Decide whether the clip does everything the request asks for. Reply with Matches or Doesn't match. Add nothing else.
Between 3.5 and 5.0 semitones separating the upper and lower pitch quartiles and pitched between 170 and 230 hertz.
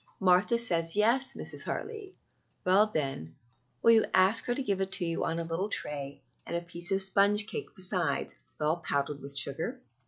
Matches